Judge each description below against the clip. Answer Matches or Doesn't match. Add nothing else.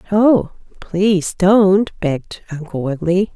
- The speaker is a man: Doesn't match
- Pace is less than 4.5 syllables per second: Matches